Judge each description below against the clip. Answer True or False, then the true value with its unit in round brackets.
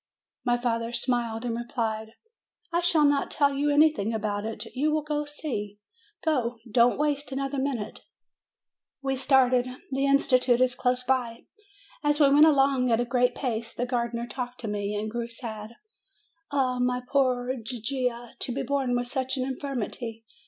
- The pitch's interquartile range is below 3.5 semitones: True (2.8 semitones)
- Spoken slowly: False (170 wpm)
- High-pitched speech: True (250 Hz)